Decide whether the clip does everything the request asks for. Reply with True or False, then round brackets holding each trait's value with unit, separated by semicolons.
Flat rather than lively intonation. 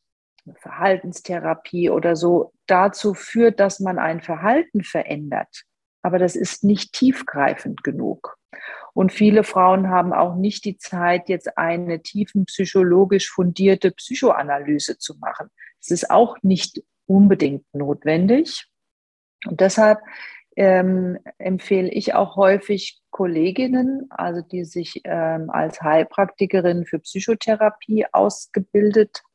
False (3.0 semitones)